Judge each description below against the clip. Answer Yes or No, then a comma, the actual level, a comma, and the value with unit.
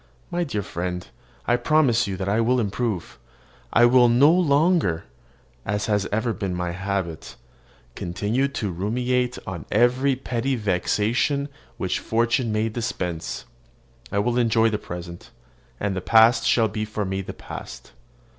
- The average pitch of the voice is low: Yes, low, 110 Hz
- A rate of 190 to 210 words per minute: No, average, 145 wpm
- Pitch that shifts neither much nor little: Yes, average, 4.3 semitones